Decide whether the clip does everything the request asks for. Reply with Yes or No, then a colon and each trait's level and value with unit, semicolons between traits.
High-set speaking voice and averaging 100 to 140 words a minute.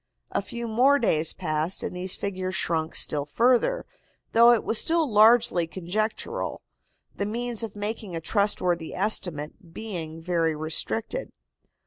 Yes: high, 195 Hz; slow, 135 wpm